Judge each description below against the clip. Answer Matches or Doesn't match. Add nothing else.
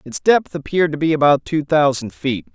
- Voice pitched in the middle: Matches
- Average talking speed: Doesn't match